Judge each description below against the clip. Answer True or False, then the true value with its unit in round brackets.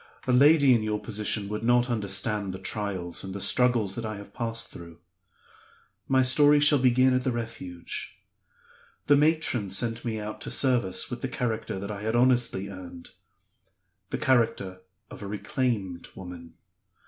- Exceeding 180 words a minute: False (160 wpm)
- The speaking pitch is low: True (110 Hz)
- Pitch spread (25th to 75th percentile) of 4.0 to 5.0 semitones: True (4.3 semitones)